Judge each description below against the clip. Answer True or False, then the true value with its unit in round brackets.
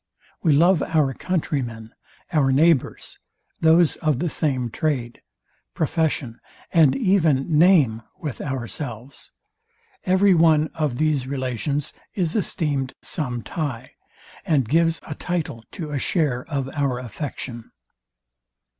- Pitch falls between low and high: True (145 Hz)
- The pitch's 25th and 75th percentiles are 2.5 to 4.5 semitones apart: True (4.1 semitones)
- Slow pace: True (120 wpm)